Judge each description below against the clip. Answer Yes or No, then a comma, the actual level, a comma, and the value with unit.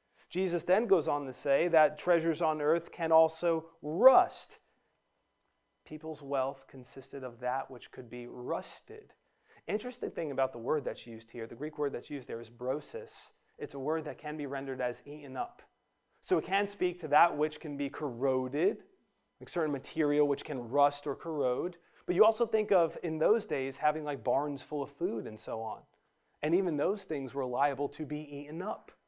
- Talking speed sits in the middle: Yes, average, 190 wpm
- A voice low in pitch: No, medium, 150 Hz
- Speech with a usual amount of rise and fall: Yes, average, 4.1 semitones